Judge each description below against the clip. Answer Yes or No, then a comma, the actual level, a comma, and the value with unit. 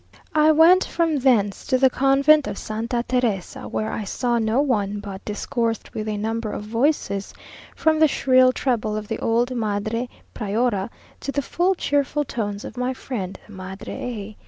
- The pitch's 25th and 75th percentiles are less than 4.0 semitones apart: No, average, 4.4 semitones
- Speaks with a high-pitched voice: Yes, high, 235 Hz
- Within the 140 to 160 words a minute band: No, average, 175 wpm